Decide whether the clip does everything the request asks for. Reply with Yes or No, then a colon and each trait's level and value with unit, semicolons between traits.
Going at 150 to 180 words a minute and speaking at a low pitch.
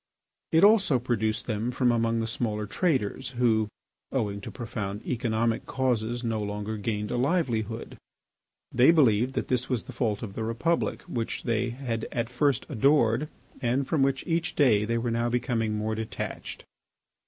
Yes: average, 165 wpm; low, 120 Hz